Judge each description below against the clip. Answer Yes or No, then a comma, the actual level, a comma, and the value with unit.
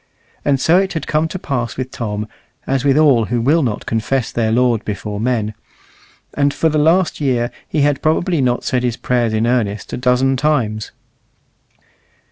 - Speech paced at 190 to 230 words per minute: No, average, 180 wpm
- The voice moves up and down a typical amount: Yes, average, 4.3 semitones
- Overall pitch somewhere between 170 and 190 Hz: No, low, 125 Hz